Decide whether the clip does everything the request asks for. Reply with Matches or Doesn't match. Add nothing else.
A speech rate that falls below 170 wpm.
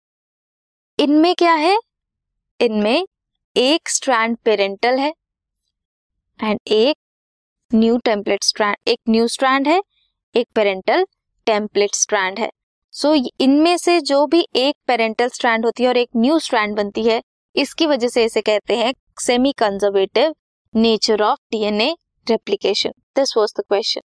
Matches